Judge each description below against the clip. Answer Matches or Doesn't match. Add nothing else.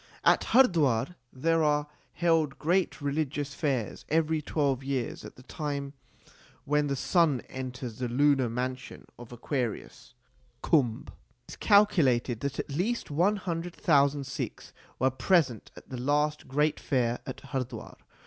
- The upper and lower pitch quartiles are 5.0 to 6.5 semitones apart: Doesn't match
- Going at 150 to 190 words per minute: Doesn't match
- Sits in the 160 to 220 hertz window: Doesn't match